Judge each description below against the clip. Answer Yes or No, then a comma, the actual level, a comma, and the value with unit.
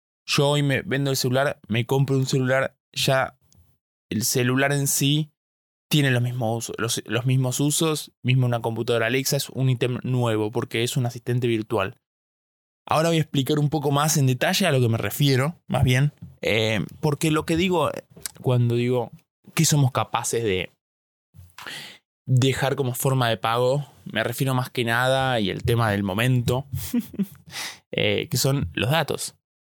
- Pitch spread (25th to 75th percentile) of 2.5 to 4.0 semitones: Yes, average, 3.2 semitones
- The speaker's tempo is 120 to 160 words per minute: No, average, 170 wpm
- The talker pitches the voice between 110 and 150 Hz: Yes, low, 130 Hz